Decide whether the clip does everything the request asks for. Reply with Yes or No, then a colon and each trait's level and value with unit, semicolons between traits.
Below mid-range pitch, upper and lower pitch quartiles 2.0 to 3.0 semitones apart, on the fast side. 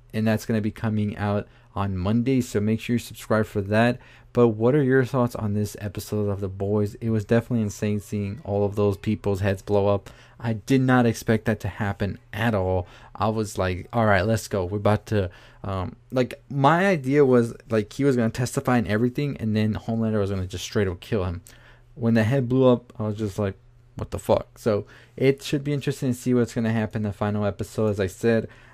Yes: low, 110 Hz; average, 2.7 semitones; fast, 235 wpm